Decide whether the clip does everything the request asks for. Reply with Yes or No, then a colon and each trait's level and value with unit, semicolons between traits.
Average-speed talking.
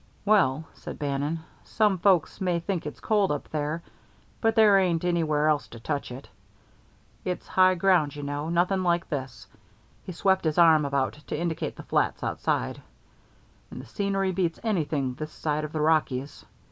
Yes: average, 170 wpm